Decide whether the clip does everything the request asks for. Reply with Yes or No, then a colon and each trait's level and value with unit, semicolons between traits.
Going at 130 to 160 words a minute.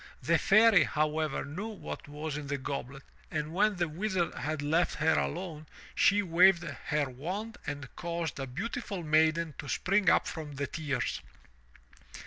Yes: average, 155 wpm